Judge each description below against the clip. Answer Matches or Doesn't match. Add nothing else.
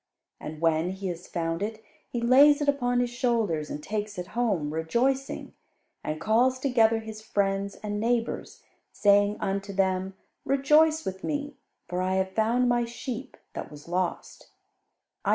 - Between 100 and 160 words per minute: Matches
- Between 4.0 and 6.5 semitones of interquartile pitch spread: Matches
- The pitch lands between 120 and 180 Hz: Doesn't match